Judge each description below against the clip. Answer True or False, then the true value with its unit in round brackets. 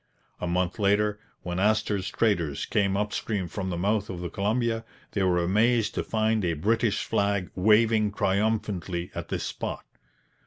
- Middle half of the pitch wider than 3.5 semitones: False (2.9 semitones)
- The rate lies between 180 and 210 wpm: False (160 wpm)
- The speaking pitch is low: True (100 Hz)